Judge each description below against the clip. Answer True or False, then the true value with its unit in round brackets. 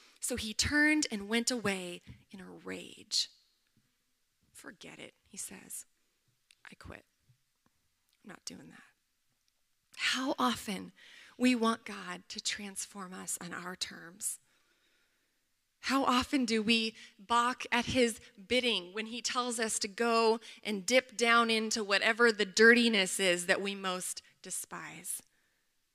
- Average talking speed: False (130 wpm)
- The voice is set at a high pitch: True (225 Hz)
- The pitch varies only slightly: False (3.5 semitones)